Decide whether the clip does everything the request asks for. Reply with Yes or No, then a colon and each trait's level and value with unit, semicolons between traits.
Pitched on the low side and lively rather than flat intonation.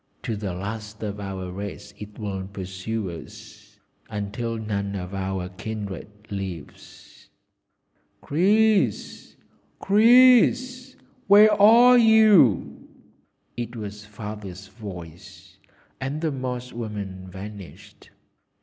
Yes: low, 105 Hz; wide, 7.7 semitones